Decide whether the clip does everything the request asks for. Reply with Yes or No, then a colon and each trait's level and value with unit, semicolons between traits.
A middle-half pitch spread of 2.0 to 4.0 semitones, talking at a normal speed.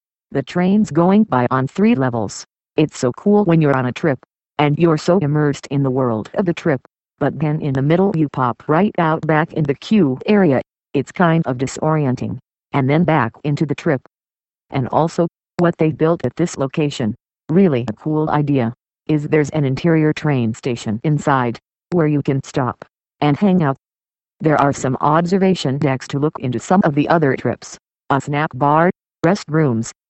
Yes: average, 3.7 semitones; average, 185 wpm